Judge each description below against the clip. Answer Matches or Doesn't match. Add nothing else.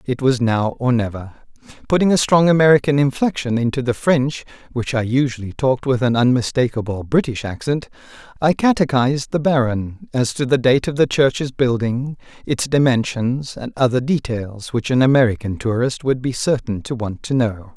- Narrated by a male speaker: Matches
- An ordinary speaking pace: Matches